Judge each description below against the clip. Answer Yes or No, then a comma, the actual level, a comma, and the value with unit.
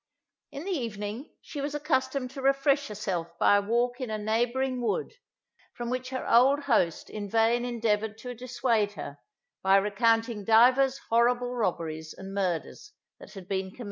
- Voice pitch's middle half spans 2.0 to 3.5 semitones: No, average, 4.0 semitones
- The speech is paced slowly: No, average, 170 wpm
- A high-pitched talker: Yes, high, 235 Hz